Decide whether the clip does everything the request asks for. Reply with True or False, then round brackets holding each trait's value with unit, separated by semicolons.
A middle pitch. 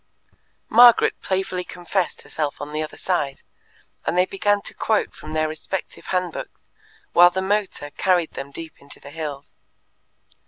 True (175 Hz)